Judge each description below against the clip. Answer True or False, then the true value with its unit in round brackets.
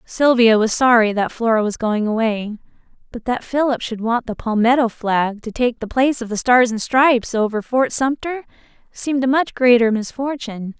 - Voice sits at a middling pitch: False (235 Hz)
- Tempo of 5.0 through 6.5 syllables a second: True (5.1 syllables/s)